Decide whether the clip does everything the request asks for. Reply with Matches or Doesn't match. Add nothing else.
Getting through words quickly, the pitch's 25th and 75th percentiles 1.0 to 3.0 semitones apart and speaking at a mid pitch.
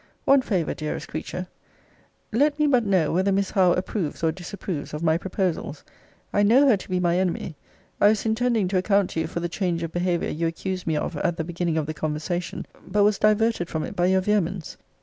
Doesn't match